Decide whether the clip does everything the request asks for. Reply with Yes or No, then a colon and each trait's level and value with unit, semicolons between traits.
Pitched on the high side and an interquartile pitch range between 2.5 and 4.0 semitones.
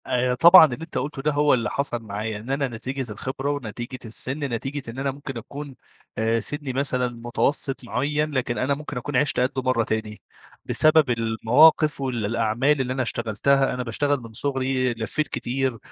No: low, 130 Hz; average, 3.3 semitones